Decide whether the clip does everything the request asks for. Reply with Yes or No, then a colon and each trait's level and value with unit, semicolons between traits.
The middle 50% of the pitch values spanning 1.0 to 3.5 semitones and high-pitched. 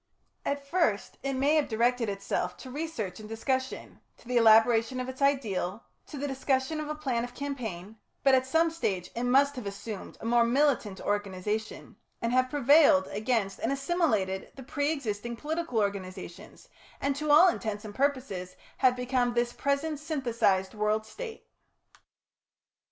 No: average, 4.7 semitones; high, 245 Hz